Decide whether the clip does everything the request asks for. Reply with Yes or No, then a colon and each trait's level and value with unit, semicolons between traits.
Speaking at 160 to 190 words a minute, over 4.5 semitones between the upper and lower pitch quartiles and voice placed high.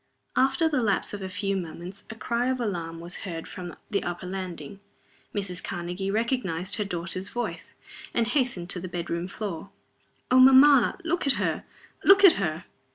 Yes: average, 170 wpm; wide, 5.4 semitones; high, 195 Hz